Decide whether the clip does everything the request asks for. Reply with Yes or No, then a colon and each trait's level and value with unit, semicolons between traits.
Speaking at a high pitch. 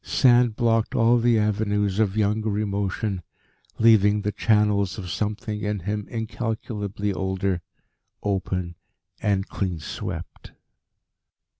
No: low, 105 Hz